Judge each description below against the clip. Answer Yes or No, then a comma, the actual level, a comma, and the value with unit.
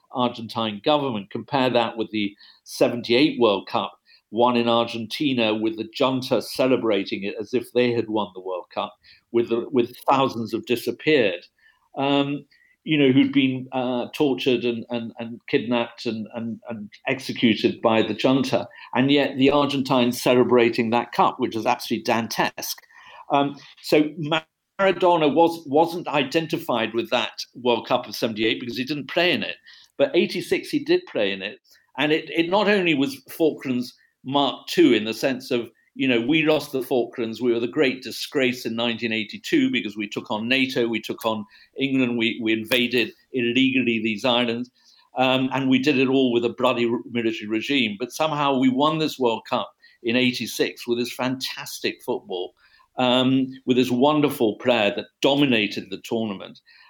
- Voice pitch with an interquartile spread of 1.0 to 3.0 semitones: No, average, 3.5 semitones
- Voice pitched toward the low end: Yes, low, 125 Hz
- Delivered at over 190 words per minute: No, average, 165 wpm